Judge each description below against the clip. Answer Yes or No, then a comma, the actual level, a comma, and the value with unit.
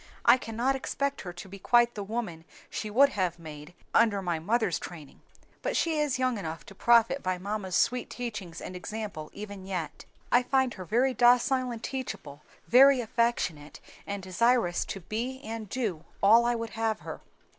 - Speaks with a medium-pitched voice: No, high, 220 Hz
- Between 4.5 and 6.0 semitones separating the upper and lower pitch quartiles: Yes, average, 4.9 semitones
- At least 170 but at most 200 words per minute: Yes, average, 175 wpm